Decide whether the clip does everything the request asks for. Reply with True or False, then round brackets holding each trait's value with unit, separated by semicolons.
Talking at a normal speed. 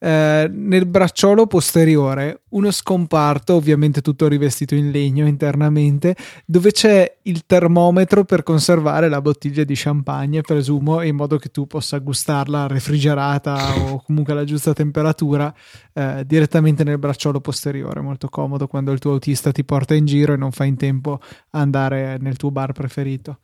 True (160 wpm)